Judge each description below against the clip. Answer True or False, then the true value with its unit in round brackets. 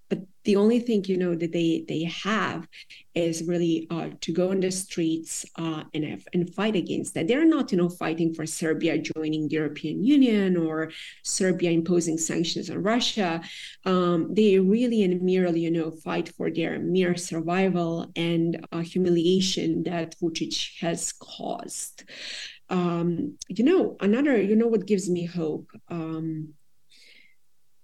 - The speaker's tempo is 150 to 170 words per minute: True (155 wpm)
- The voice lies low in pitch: False (175 Hz)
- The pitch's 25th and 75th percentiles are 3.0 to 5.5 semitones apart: False (2.6 semitones)